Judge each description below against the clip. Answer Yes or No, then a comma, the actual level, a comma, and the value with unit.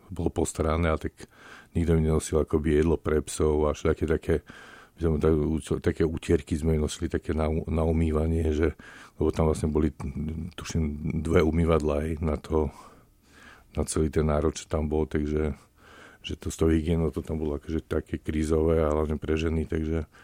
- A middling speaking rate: No, fast, 180 wpm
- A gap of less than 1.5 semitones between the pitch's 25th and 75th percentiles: Yes, narrow, 1.1 semitones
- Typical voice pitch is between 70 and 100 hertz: Yes, very low, 80 Hz